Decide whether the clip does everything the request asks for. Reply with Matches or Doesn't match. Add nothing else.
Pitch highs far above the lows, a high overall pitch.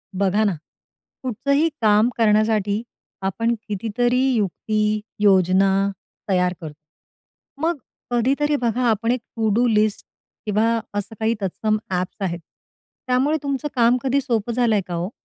Doesn't match